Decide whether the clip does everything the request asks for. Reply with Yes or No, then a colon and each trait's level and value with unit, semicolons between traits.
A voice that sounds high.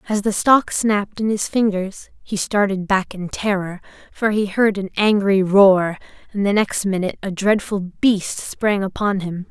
Yes: high, 200 Hz